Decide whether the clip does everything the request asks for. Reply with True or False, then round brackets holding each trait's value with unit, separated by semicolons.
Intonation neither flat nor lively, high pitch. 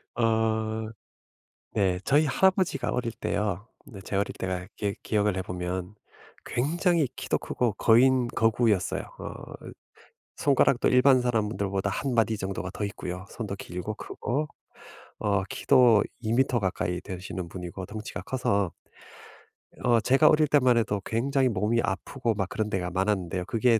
False (4.4 semitones; 110 Hz)